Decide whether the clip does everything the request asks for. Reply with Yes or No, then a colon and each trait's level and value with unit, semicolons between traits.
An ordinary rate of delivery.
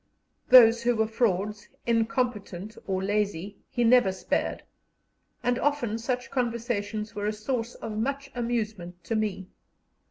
No: slow, 130 wpm